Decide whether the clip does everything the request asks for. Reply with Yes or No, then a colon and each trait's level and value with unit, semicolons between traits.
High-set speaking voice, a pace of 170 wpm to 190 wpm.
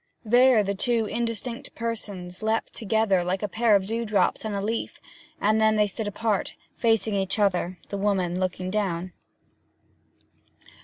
No: high, 210 Hz; average, 150 wpm